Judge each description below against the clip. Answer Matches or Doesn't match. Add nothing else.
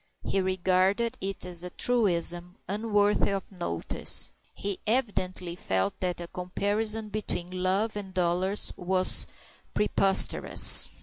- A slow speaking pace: Matches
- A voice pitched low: Doesn't match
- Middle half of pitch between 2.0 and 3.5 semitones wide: Matches